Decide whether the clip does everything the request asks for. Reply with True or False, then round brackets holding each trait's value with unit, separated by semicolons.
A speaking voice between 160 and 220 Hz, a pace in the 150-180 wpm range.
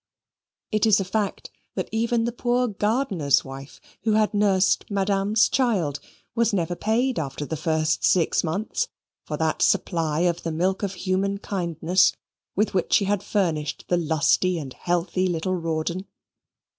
True (185 Hz; 155 wpm)